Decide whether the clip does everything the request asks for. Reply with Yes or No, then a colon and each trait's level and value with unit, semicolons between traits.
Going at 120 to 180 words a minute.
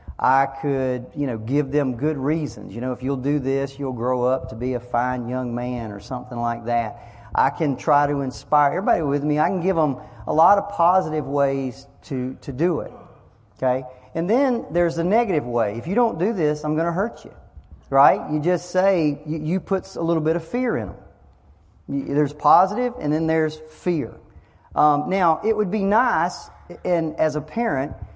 No: average, 200 wpm